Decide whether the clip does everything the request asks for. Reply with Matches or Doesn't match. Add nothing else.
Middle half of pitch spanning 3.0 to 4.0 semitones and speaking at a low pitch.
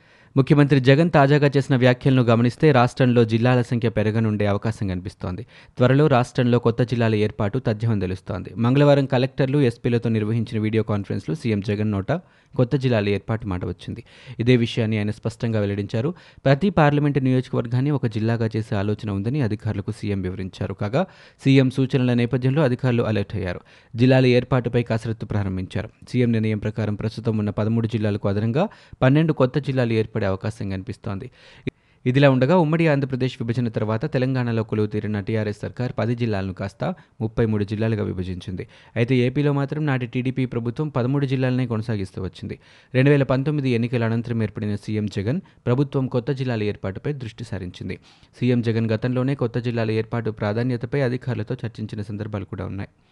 Matches